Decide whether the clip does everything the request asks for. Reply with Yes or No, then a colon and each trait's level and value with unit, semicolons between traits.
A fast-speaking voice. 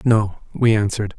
No: average, 150 wpm